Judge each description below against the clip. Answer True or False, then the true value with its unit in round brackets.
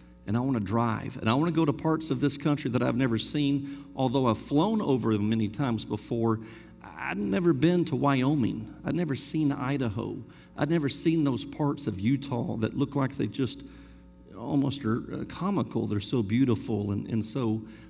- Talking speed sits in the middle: True (190 wpm)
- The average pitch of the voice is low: True (130 Hz)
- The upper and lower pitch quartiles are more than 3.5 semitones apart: True (4.3 semitones)